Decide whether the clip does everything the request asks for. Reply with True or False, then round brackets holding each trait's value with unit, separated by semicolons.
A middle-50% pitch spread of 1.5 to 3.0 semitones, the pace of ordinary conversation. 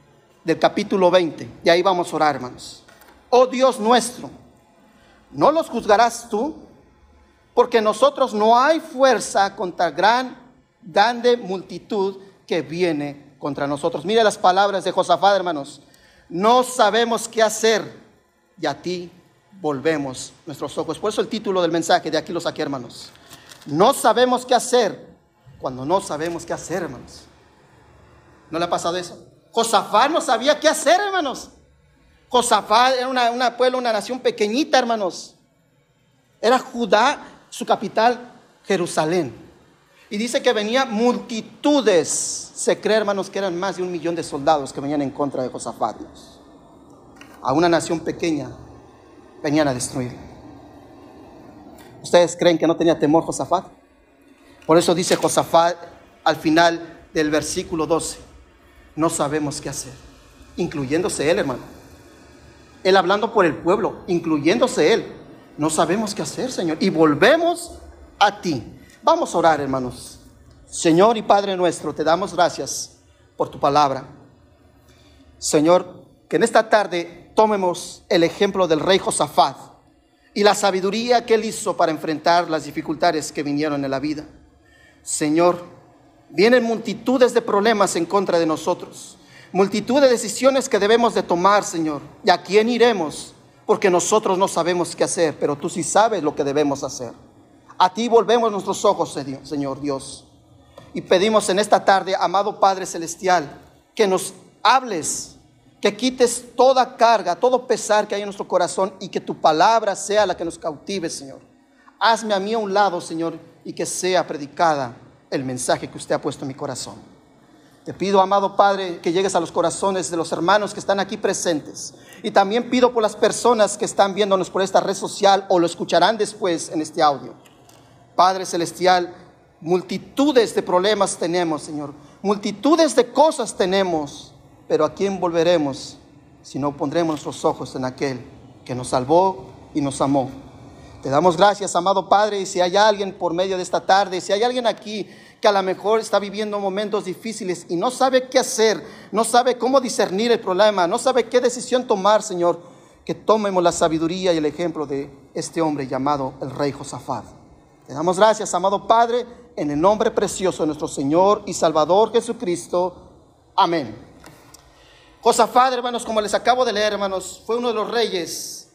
False (5.4 semitones; 160 wpm)